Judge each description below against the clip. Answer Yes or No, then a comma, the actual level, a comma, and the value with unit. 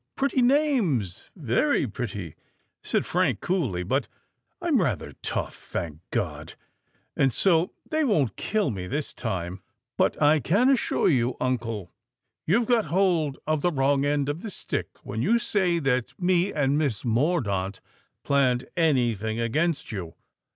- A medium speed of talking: Yes, average, 145 wpm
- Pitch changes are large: Yes, wide, 7.9 semitones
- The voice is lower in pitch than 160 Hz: Yes, medium, 140 Hz